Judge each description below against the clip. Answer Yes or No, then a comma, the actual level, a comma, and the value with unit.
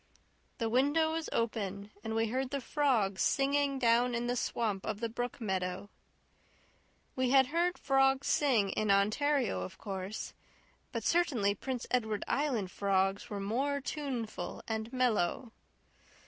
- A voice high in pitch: Yes, high, 235 Hz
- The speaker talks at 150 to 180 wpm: No, average, 140 wpm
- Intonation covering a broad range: No, average, 4.9 semitones